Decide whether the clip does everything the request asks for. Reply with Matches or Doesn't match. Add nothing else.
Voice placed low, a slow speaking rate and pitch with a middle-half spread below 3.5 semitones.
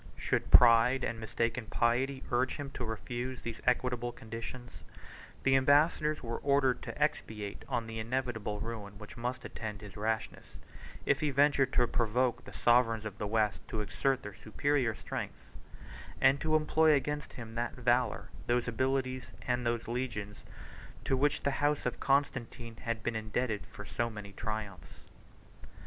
Doesn't match